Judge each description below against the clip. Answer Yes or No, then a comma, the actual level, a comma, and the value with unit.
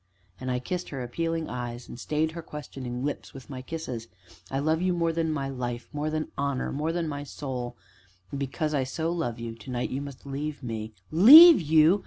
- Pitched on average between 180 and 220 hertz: No, medium, 140 Hz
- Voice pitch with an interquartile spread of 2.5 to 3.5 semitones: No, average, 4.2 semitones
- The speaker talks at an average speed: No, fast, 215 wpm